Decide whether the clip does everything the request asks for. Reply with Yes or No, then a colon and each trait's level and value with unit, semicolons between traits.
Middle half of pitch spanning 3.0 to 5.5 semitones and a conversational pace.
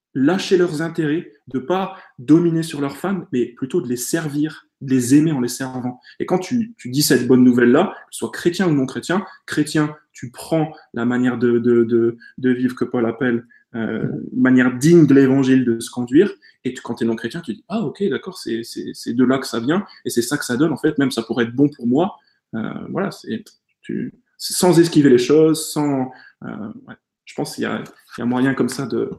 No: average, 5.1 semitones; fast, 230 wpm